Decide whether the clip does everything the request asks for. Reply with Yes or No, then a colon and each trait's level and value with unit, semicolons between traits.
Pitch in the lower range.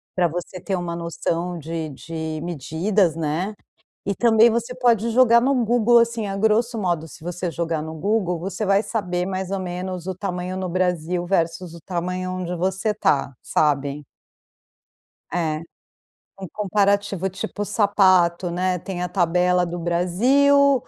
No: medium, 185 Hz